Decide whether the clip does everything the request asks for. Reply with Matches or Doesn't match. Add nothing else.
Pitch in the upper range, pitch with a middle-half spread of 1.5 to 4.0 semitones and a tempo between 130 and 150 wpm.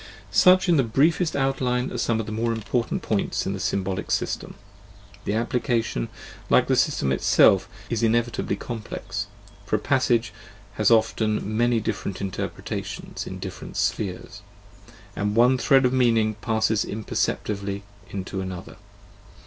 Doesn't match